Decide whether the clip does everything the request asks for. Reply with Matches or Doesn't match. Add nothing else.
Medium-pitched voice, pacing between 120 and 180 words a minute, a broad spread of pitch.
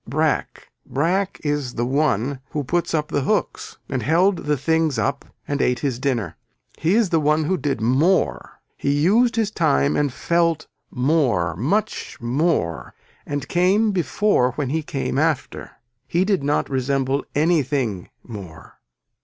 Doesn't match